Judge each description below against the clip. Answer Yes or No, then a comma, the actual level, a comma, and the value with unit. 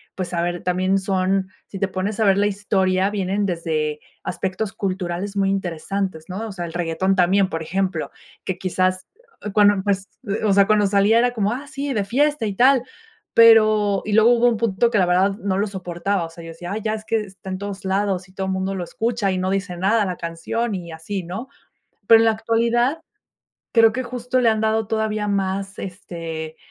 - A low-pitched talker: No, high, 195 Hz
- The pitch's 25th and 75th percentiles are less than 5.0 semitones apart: Yes, average, 2.8 semitones